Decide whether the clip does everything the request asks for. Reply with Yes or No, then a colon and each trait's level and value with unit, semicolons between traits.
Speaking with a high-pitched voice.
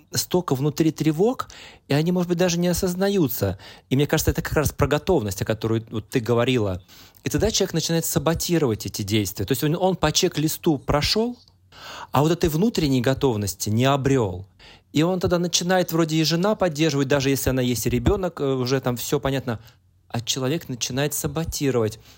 No: medium, 140 Hz